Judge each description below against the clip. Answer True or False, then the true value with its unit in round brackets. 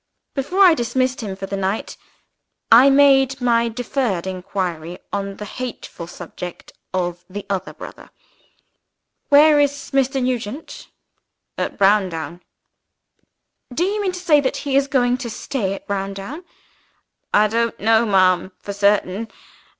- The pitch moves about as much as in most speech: False (5.7 semitones)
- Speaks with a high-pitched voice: True (225 Hz)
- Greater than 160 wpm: False (135 wpm)